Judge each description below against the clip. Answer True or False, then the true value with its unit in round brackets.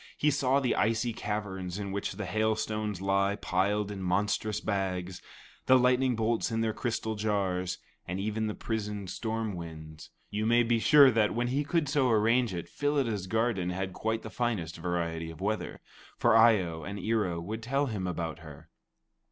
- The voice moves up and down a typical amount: True (3.7 semitones)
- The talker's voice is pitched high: False (105 Hz)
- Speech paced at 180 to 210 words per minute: True (185 wpm)